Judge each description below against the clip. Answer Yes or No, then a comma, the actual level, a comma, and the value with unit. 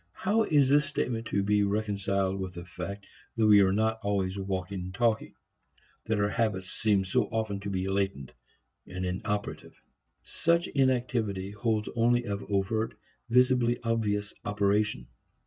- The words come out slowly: No, average, 145 wpm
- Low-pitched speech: Yes, low, 105 Hz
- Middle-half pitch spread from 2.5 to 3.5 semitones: Yes, average, 2.8 semitones